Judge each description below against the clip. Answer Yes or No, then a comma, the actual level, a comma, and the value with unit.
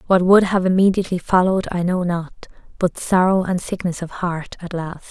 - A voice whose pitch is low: No, medium, 180 Hz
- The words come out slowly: No, average, 190 wpm